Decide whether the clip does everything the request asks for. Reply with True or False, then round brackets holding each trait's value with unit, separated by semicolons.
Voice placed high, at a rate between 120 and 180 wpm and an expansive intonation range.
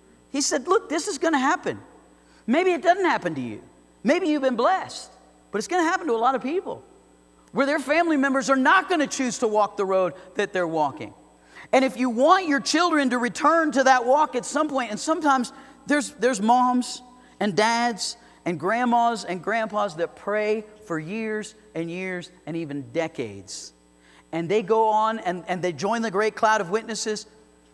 False (235 Hz; 195 wpm; 6.2 semitones)